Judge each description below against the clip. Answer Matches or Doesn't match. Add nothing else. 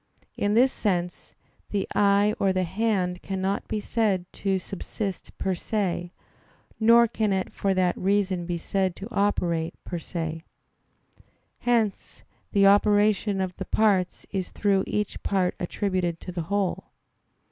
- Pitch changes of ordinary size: Doesn't match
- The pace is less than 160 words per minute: Matches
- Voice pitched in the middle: Doesn't match